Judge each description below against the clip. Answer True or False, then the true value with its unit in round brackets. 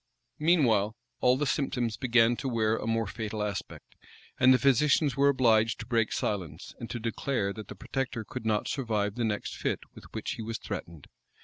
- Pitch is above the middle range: False (115 Hz)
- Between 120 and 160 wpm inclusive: False (190 wpm)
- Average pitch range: True (3.1 semitones)